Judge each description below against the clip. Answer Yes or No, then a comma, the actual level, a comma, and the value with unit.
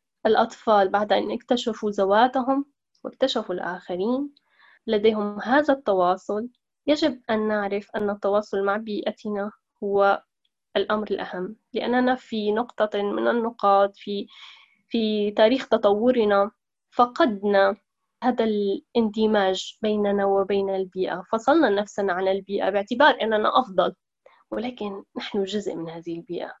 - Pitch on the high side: Yes, high, 210 Hz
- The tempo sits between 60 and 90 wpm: No, average, 110 wpm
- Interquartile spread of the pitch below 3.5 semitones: Yes, average, 2.9 semitones